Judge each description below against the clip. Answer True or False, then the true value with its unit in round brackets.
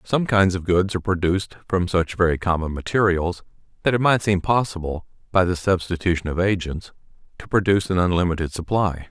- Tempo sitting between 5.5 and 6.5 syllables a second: True (5.8 syllables/s)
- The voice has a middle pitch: False (90 Hz)